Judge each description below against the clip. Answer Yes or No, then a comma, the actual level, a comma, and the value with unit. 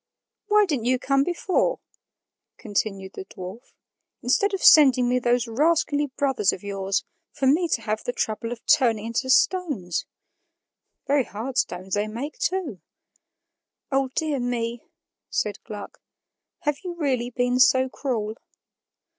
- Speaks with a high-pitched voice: Yes, very high, 250 Hz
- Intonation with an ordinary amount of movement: Yes, average, 4.8 semitones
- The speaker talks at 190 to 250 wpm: No, average, 140 wpm